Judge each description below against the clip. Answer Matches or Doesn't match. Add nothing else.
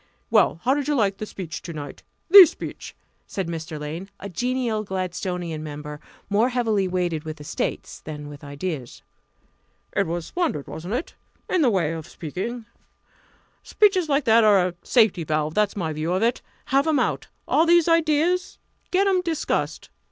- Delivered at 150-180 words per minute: Matches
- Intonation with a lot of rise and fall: Matches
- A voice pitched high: Matches